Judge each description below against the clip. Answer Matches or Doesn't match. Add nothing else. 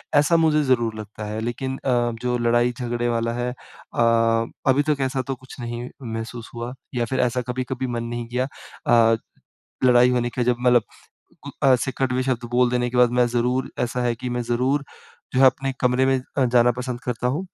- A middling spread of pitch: Doesn't match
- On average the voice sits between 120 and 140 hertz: Matches